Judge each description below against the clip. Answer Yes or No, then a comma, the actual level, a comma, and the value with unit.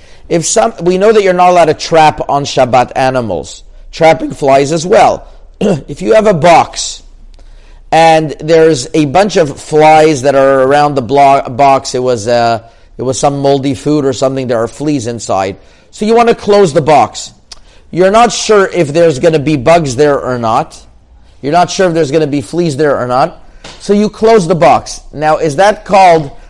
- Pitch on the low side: No, medium, 155 Hz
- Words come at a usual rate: Yes, average, 195 wpm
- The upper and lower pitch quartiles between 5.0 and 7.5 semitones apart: No, average, 4.4 semitones